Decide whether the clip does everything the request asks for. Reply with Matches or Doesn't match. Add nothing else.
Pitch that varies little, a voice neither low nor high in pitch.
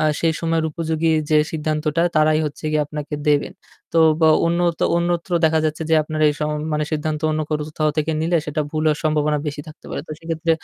Matches